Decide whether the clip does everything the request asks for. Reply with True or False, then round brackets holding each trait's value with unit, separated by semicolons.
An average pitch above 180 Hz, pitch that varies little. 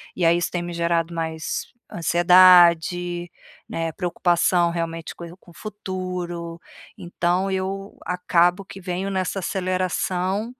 False (175 Hz; 1.5 semitones)